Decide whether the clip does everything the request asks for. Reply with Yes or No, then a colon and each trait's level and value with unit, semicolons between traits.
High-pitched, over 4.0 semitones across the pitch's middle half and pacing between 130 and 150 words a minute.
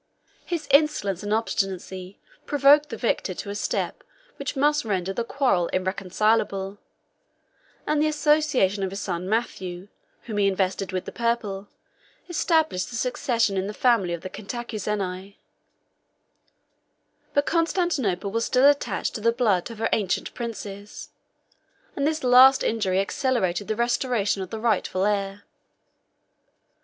Yes: high, 215 Hz; average, 4.7 semitones; slow, 135 wpm